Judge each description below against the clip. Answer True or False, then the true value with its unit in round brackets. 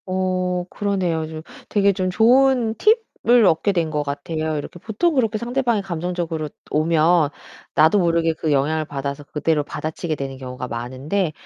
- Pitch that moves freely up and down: False (4.7 semitones)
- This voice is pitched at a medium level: True (165 Hz)